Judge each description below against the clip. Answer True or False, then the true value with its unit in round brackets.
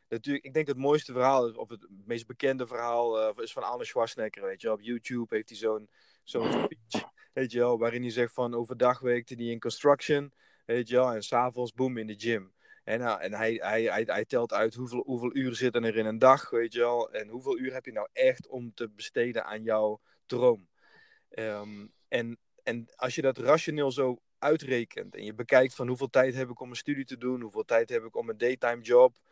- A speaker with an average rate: False (225 wpm)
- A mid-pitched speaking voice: False (125 Hz)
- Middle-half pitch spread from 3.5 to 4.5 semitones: False (2.7 semitones)